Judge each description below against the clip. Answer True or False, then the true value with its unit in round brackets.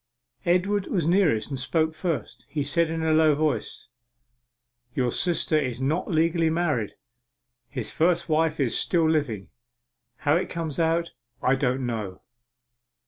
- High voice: False (155 Hz)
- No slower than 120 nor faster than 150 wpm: True (140 wpm)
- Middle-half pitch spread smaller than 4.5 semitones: True (3.9 semitones)